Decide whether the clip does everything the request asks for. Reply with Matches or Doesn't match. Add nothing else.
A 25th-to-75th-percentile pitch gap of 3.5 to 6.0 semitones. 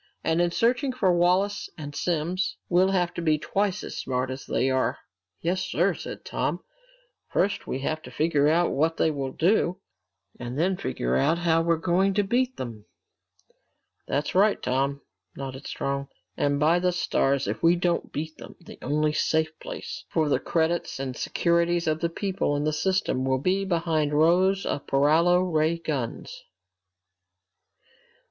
Matches